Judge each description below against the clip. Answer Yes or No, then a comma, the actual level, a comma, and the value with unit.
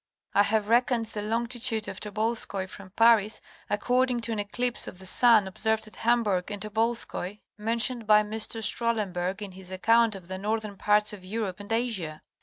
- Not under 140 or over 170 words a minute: No, average, 180 wpm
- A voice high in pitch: Yes, high, 215 Hz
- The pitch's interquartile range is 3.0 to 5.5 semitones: No, narrow, 2.4 semitones